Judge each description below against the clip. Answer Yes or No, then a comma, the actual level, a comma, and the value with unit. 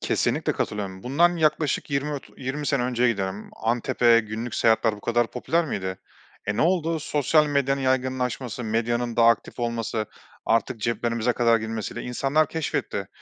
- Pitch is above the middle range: No, low, 120 Hz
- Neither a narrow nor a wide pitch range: Yes, average, 3.6 semitones